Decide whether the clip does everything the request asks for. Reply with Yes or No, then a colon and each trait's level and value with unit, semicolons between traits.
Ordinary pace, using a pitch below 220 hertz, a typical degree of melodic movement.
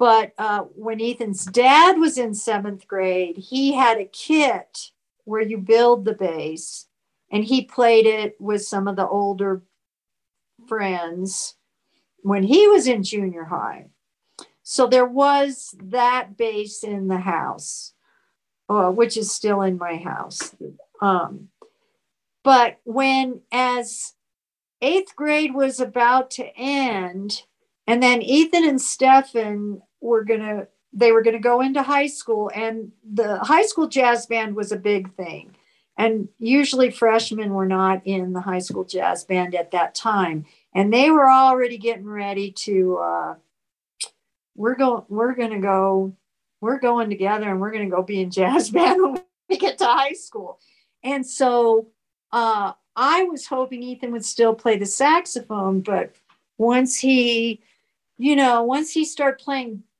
No: average, 150 wpm; high, 225 Hz; average, 4.6 semitones